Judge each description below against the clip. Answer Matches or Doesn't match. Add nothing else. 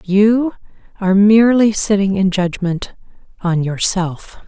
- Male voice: Doesn't match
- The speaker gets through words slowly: Matches